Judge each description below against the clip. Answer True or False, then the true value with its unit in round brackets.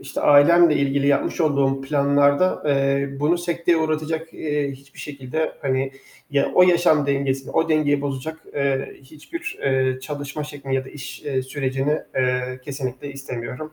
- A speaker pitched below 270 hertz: True (140 Hz)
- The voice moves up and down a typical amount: False (2.3 semitones)